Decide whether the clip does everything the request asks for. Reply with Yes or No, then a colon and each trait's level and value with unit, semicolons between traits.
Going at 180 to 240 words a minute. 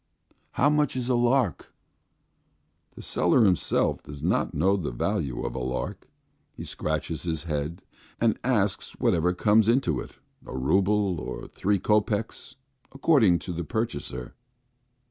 No: average, 140 wpm